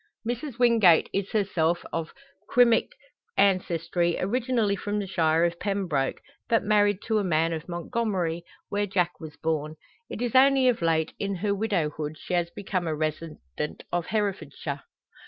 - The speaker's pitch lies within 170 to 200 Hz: Yes, medium, 185 Hz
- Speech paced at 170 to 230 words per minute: No, average, 155 wpm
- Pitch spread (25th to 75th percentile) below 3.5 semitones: No, average, 4.5 semitones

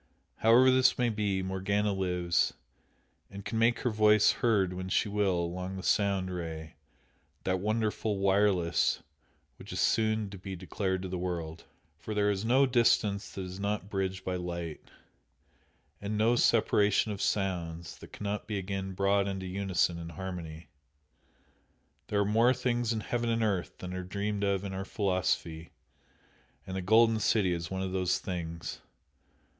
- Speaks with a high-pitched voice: No, very low, 95 Hz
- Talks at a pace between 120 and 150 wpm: No, average, 160 wpm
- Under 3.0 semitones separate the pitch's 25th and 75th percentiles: Yes, narrow, 2.5 semitones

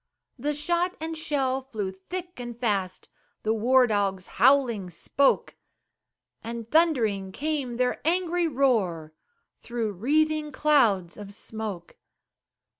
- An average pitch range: No, wide, 6.7 semitones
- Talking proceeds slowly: Yes, slow, 115 wpm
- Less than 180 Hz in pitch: No, high, 245 Hz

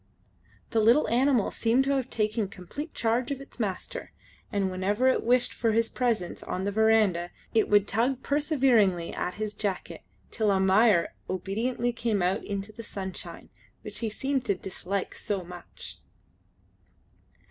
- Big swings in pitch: No, average, 4.0 semitones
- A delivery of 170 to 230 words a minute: No, average, 150 wpm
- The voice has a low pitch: No, high, 215 Hz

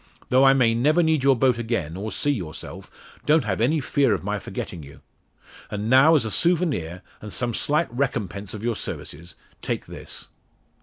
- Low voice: Yes, low, 120 Hz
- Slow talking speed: No, average, 185 wpm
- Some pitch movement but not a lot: No, wide, 5.7 semitones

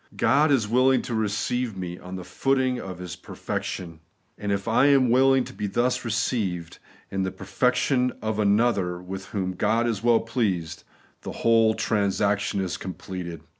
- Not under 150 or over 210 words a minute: Yes, average, 170 wpm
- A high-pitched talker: No, low, 105 Hz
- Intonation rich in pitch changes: No, average, 4.3 semitones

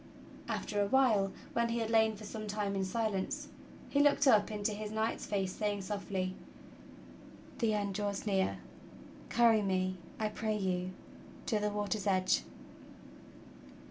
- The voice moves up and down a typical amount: No, narrow, 2.0 semitones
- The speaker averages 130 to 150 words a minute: Yes, average, 145 wpm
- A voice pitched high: Yes, high, 210 Hz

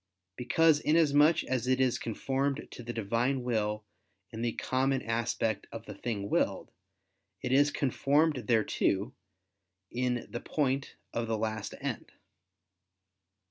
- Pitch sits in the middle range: No, low, 125 Hz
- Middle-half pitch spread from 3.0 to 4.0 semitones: Yes, average, 3.3 semitones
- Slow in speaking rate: Yes, slow, 130 wpm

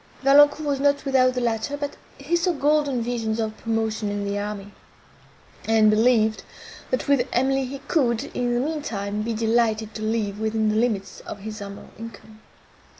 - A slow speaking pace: No, average, 175 wpm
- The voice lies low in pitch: No, high, 230 Hz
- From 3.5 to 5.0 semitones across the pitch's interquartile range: Yes, average, 3.9 semitones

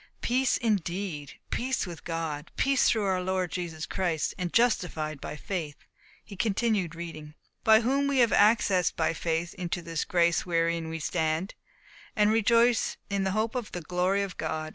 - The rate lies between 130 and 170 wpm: Yes, average, 165 wpm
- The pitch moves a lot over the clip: No, average, 4.8 semitones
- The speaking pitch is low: No, medium, 180 Hz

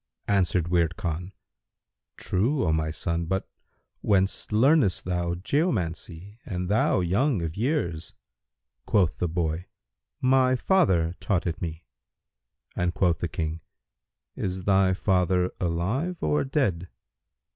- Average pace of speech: No, slow, 125 wpm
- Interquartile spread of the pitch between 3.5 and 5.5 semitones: Yes, average, 4.0 semitones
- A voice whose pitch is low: Yes, very low, 90 Hz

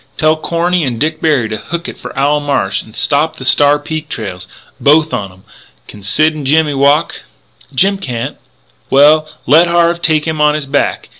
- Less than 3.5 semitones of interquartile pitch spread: Yes, average, 2.9 semitones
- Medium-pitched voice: Yes, medium, 150 Hz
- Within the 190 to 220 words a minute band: Yes, average, 195 wpm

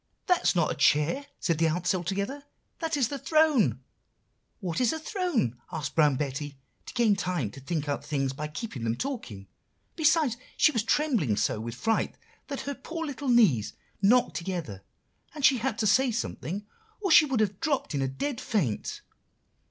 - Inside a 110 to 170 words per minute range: No, average, 185 wpm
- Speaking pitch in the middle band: No, high, 205 Hz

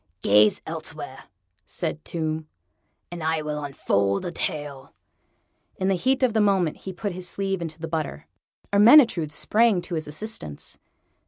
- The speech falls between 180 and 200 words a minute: No, average, 150 wpm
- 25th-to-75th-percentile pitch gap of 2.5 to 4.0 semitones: No, average, 4.5 semitones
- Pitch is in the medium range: Yes, medium, 165 Hz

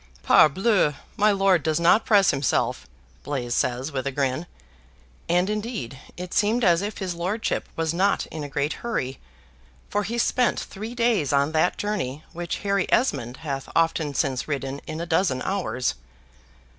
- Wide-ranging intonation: Yes, wide, 6.3 semitones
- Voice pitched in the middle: Yes, medium, 170 Hz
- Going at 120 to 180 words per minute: Yes, average, 160 wpm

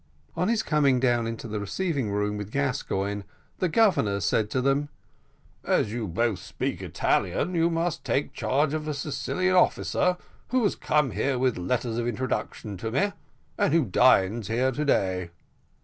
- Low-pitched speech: Yes, low, 130 Hz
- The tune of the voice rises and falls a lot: Yes, wide, 6.6 semitones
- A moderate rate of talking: Yes, average, 170 wpm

